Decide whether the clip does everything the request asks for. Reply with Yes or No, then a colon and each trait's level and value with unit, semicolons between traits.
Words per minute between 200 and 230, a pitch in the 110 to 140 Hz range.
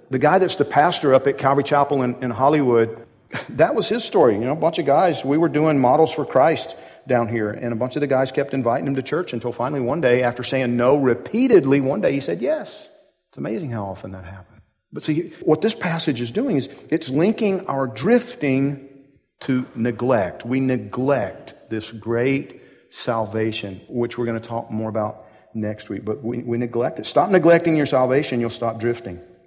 Yes: fast, 205 wpm; low, 130 Hz